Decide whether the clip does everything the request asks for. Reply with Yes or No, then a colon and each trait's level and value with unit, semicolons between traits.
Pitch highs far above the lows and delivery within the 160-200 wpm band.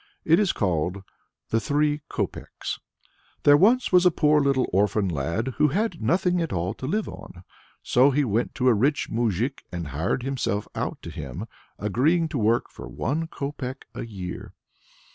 Yes: wide, 7.0 semitones; average, 170 wpm